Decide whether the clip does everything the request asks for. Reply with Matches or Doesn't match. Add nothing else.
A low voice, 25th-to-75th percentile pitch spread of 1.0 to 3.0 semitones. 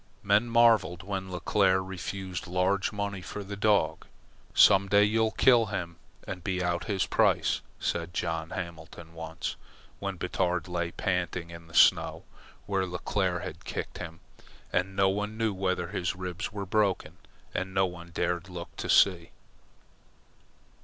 Matches